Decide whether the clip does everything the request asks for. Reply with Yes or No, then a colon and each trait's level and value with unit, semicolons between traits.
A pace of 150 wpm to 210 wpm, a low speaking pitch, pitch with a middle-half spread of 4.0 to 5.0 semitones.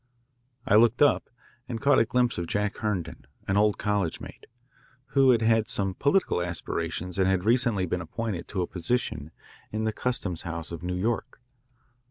Yes: average, 175 wpm; low, 105 Hz; average, 4.5 semitones